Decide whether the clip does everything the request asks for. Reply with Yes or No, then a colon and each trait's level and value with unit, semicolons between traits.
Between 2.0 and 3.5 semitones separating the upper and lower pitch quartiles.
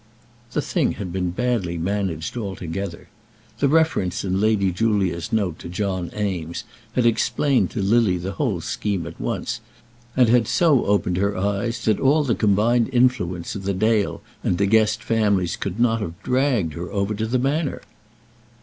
No: average, 4.3 semitones